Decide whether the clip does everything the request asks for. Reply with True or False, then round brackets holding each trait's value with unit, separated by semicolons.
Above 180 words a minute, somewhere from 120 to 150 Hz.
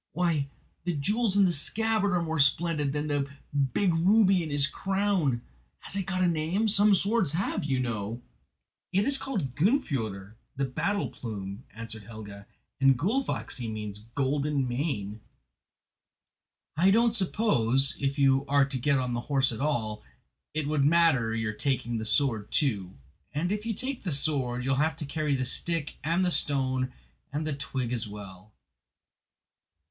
False (165 wpm; 140 Hz)